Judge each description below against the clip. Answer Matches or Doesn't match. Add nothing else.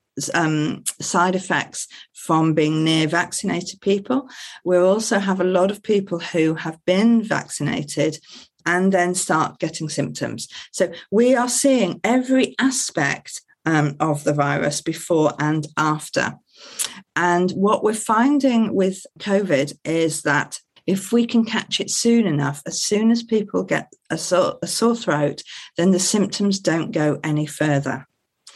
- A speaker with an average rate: Matches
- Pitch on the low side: Doesn't match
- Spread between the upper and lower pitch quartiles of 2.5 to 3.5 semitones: Doesn't match